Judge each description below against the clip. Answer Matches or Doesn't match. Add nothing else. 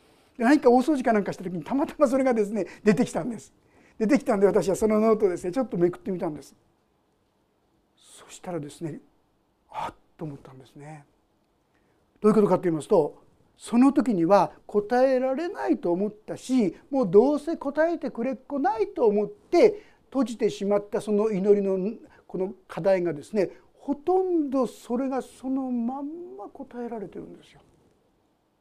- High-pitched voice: Matches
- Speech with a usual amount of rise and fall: Doesn't match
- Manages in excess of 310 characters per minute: Matches